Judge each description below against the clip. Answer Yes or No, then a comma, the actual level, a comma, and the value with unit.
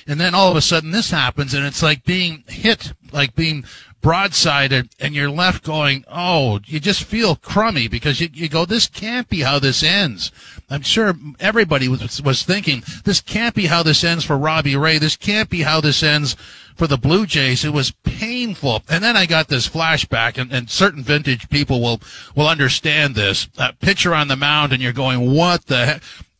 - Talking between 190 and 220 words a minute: Yes, average, 200 wpm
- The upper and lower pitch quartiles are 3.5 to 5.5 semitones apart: Yes, average, 4.2 semitones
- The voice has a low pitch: No, medium, 150 Hz